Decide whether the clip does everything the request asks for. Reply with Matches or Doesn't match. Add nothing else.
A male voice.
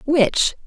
Doesn't match